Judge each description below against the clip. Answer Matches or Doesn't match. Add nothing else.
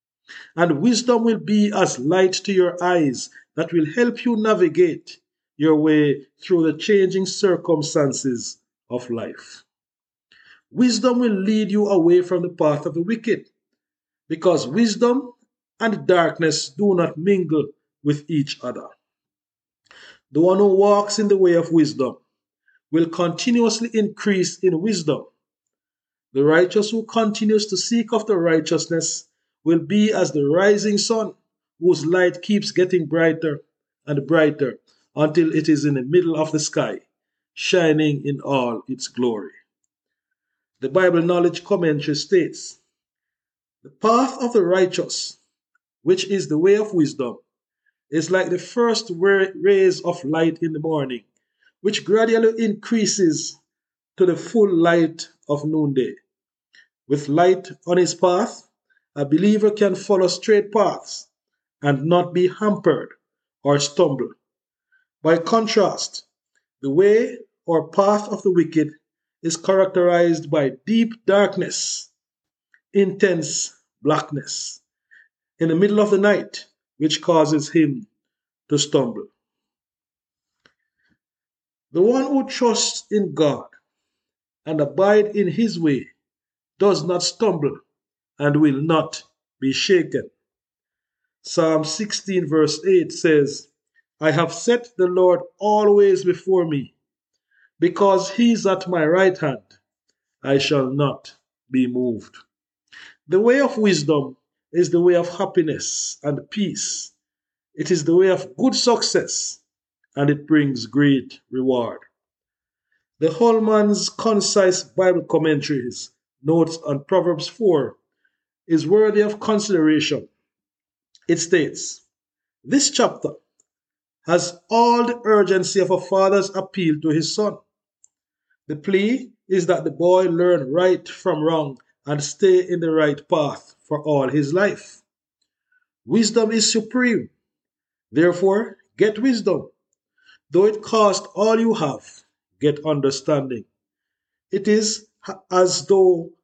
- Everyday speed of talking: Doesn't match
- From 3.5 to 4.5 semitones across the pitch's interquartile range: Doesn't match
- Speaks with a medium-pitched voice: Matches